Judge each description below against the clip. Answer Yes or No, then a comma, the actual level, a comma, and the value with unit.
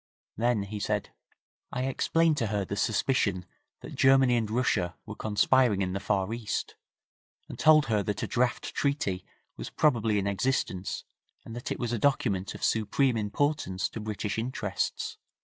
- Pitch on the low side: Yes, low, 110 Hz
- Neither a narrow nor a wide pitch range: Yes, average, 4.3 semitones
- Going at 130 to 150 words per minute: No, average, 165 wpm